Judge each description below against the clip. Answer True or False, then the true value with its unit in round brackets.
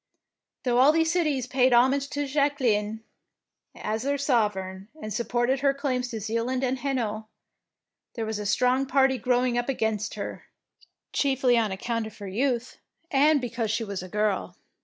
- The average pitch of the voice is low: False (245 Hz)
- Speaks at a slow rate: False (160 wpm)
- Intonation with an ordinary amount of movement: True (3.7 semitones)